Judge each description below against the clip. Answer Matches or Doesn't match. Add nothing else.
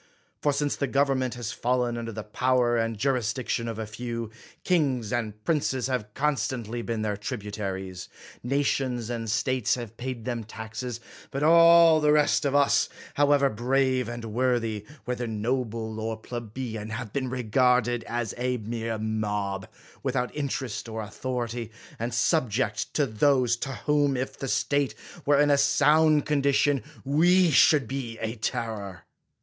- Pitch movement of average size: Matches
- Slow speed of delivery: Doesn't match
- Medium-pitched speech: Doesn't match